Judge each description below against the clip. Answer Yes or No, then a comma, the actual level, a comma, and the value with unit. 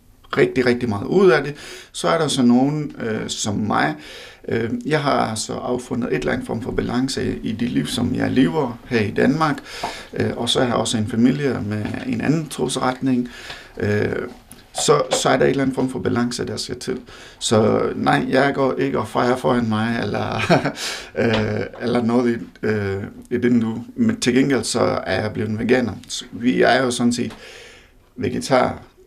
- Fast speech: No, average, 185 wpm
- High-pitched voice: No, low, 125 Hz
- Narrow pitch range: Yes, narrow, 2.1 semitones